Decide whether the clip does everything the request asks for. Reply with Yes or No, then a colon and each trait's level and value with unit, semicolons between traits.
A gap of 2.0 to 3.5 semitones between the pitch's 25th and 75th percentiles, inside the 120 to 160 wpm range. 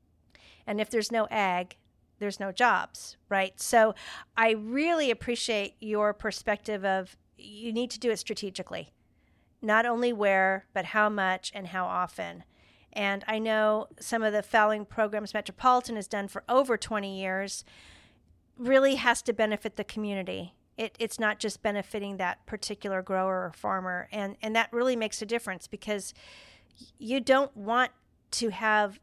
Yes: average, 2.8 semitones; average, 155 wpm